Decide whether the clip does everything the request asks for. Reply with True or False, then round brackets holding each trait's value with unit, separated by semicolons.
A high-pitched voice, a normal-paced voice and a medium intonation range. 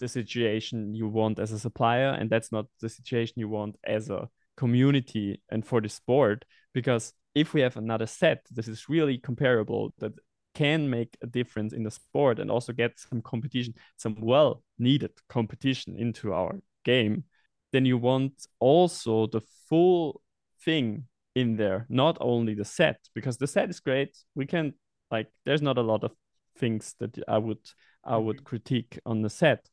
False (120 Hz; 175 wpm; 3.3 semitones)